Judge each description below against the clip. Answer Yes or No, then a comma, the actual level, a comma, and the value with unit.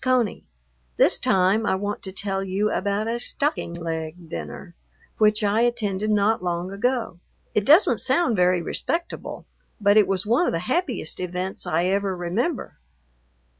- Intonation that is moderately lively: Yes, average, 3.7 semitones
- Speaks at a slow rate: No, average, 155 wpm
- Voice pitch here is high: Yes, high, 200 Hz